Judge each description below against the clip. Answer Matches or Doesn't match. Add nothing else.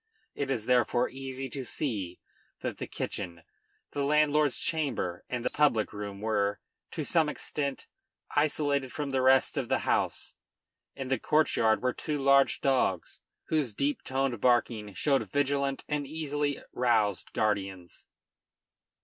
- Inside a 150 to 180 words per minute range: Doesn't match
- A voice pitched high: Doesn't match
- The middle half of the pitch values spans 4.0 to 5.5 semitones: Matches